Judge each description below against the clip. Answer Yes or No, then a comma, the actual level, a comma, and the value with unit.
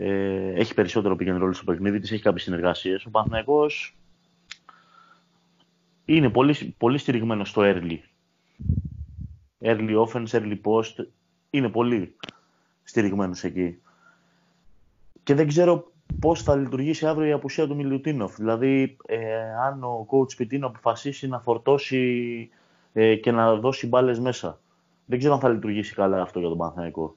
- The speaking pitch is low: Yes, low, 115 Hz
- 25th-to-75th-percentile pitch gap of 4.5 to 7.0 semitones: Yes, wide, 5.5 semitones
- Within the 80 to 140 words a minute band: Yes, average, 135 wpm